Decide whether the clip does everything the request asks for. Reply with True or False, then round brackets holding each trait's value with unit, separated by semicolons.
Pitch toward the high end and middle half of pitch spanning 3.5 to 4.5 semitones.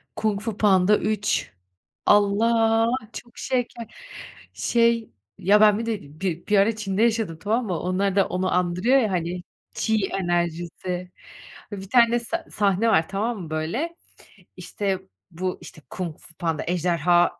True (200 Hz; 4.0 semitones)